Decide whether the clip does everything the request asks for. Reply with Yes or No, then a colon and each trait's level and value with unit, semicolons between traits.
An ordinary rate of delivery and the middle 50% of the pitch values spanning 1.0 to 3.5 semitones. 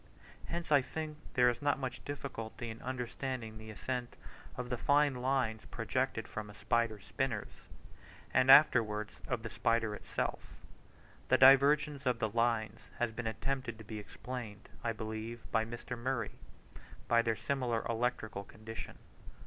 Yes: average, 150 wpm; average, 2.8 semitones